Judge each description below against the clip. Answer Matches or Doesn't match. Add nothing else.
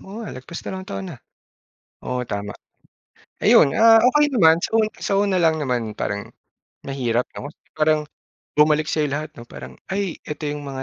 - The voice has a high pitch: Doesn't match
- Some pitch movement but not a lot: Doesn't match